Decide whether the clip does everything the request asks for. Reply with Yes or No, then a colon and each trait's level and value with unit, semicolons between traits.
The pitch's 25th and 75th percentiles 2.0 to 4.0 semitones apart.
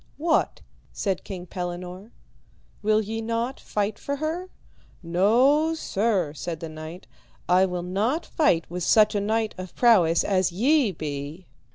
No: average, 4.7 semitones